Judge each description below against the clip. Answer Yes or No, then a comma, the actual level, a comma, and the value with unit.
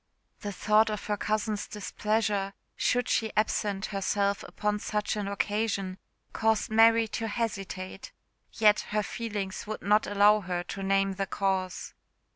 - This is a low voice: No, high, 210 Hz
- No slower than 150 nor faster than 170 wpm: No, average, 140 wpm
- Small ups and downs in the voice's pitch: Yes, narrow, 1.7 semitones